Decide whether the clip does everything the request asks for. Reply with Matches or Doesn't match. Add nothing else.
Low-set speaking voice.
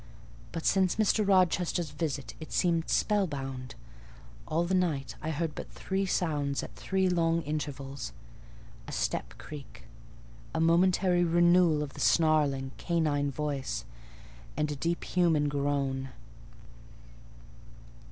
Doesn't match